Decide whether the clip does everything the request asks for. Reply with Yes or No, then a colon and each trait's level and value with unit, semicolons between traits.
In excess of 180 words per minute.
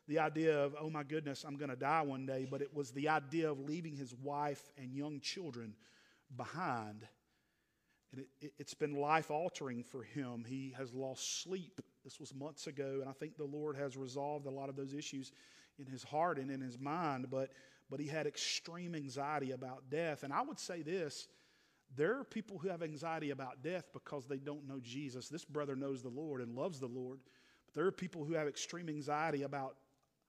Yes: fast, 205 wpm